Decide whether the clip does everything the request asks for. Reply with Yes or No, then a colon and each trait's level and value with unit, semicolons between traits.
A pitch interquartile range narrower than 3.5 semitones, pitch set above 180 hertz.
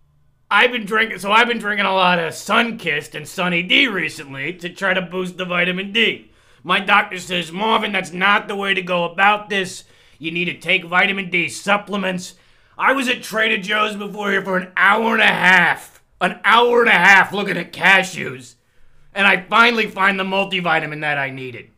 Yes: average, 2.9 semitones; high, 190 Hz